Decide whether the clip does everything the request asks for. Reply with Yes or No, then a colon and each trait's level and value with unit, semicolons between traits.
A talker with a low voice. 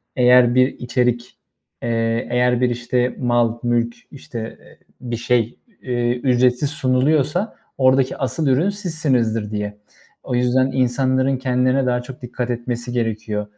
Yes: low, 125 Hz